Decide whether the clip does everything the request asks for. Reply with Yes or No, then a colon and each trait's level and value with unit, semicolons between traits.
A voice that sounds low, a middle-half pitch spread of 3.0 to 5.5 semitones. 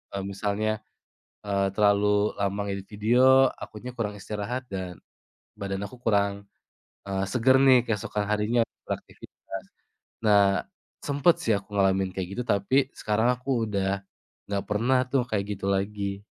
Yes: low, 105 Hz; average, 3.4 semitones